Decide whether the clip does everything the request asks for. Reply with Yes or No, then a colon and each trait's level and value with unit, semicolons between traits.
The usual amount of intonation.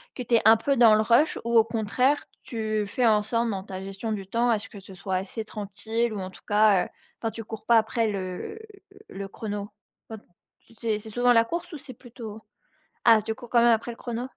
No: narrow, 2.3 semitones